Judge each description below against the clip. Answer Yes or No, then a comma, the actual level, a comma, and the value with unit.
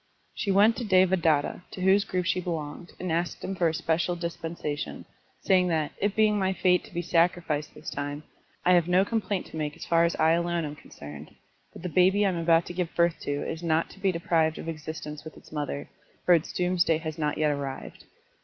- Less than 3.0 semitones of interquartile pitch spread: Yes, narrow, 2.6 semitones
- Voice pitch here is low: No, medium, 170 Hz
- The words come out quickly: Yes, fast, 220 wpm